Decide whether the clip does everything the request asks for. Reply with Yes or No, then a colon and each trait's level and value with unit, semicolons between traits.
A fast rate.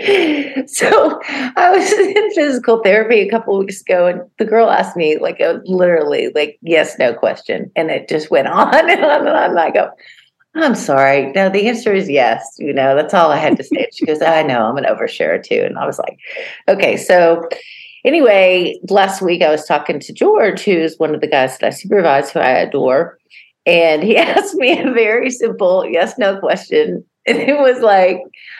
Yes: fast, 210 wpm